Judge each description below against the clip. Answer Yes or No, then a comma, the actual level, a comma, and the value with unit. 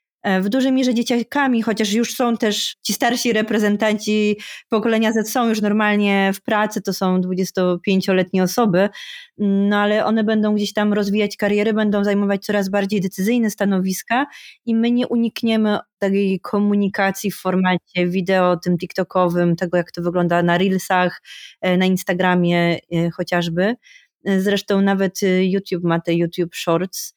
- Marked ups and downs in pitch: No, average, 2.8 semitones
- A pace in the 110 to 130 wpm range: No, average, 140 wpm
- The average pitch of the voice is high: Yes, high, 200 Hz